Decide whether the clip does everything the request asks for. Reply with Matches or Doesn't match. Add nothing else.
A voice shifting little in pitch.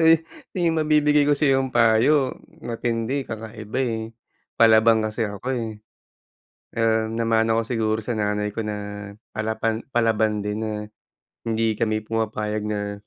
Matches